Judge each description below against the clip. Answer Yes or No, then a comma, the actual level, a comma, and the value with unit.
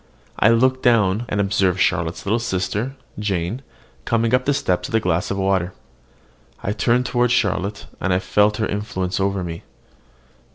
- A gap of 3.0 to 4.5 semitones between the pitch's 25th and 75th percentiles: Yes, average, 3.8 semitones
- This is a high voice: No, low, 100 Hz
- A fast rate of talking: No, average, 165 wpm